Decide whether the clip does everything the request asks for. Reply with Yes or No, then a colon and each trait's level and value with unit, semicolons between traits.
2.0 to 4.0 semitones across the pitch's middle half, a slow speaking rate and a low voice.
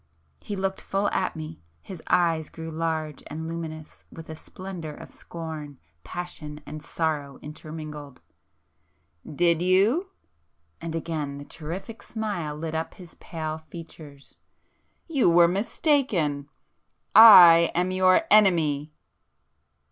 No: average, 3.2 semitones; slow, 115 wpm; medium, 165 Hz